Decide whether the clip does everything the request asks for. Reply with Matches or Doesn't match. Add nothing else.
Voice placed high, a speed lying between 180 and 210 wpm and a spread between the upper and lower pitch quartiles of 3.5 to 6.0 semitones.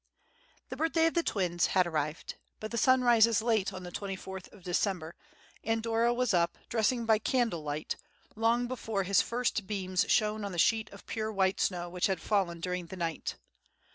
Matches